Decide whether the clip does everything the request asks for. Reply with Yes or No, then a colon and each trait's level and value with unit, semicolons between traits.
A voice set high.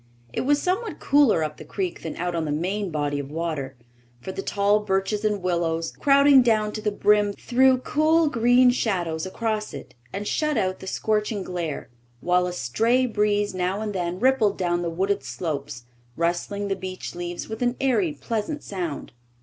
Yes: high, 200 Hz